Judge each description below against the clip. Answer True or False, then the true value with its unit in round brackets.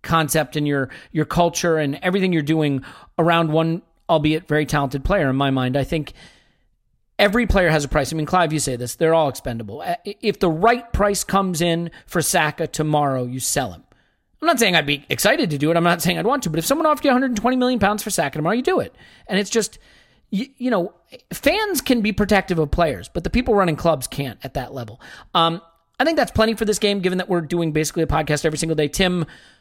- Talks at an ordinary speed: False (235 wpm)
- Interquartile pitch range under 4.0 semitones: False (4.9 semitones)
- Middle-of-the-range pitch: True (165 Hz)